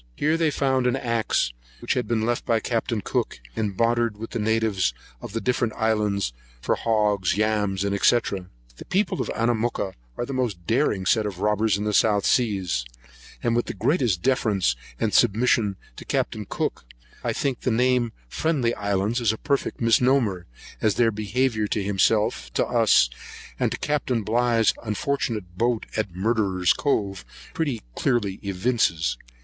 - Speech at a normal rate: Yes, average, 165 wpm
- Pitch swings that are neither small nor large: Yes, average, 3.3 semitones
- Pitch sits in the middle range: No, low, 110 Hz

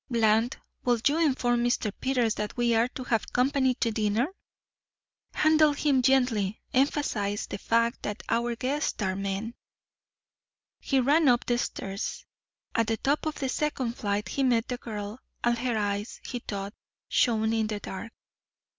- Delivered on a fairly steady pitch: No, average, 3.4 semitones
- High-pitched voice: Yes, high, 235 Hz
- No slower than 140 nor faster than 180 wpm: Yes, average, 160 wpm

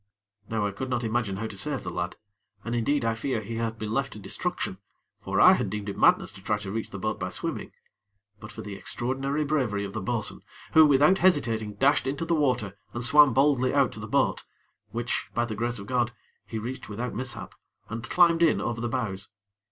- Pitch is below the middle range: Yes, low, 120 Hz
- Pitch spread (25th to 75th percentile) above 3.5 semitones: Yes, average, 4.1 semitones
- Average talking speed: No, fast, 220 wpm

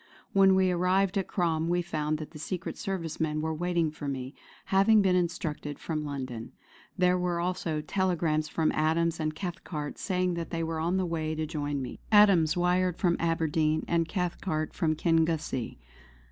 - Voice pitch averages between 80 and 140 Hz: No, medium, 165 Hz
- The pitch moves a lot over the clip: No, narrow, 2.6 semitones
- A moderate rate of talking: Yes, average, 175 wpm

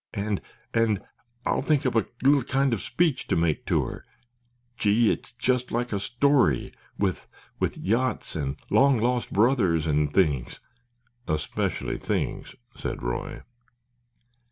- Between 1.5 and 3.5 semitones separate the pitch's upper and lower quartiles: No, average, 5.1 semitones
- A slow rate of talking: Yes, slow, 120 wpm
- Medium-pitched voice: No, low, 120 Hz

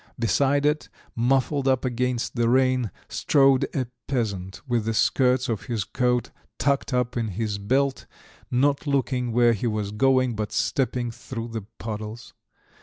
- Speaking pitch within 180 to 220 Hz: No, low, 125 Hz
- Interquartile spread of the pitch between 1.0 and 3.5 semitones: Yes, average, 2.7 semitones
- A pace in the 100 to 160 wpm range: Yes, average, 150 wpm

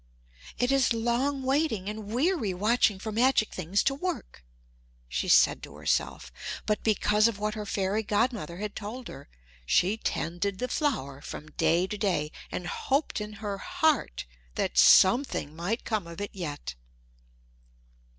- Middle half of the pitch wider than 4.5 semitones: Yes, average, 5.2 semitones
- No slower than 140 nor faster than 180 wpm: Yes, average, 150 wpm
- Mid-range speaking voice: No, high, 210 Hz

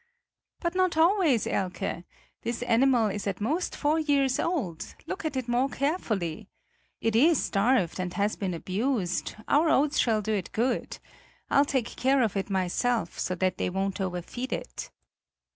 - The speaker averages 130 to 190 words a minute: Yes, average, 160 wpm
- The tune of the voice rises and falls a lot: Yes, wide, 6.4 semitones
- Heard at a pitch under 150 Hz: No, high, 235 Hz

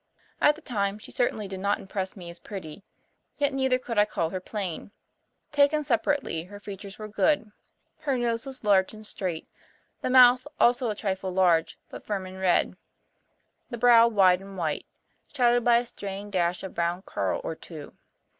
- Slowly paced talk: No, average, 180 wpm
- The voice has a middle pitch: No, high, 205 Hz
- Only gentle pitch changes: No, average, 4.4 semitones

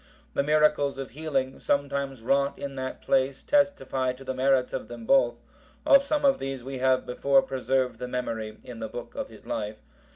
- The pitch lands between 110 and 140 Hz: Yes, low, 135 Hz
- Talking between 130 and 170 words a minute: No, average, 190 wpm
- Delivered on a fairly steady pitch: Yes, narrow, 1.9 semitones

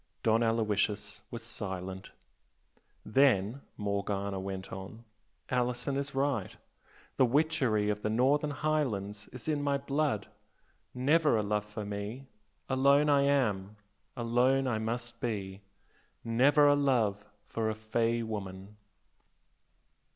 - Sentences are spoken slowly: Yes, slow, 120 wpm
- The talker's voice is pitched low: Yes, low, 115 Hz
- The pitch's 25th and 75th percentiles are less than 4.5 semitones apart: No, average, 4.8 semitones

